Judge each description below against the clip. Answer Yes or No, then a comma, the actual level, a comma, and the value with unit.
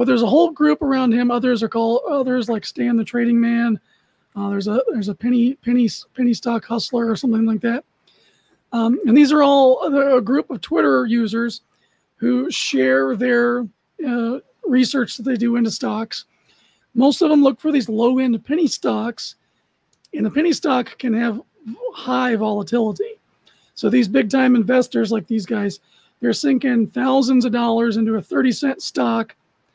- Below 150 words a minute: No, average, 175 wpm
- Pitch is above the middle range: Yes, high, 240 Hz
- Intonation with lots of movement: No, narrow, 2.6 semitones